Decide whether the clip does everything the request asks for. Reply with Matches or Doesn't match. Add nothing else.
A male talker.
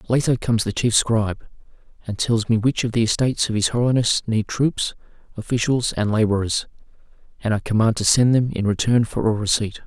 Matches